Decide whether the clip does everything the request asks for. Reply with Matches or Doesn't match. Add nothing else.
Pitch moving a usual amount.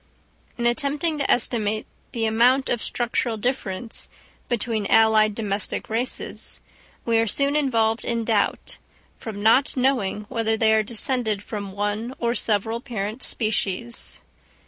Doesn't match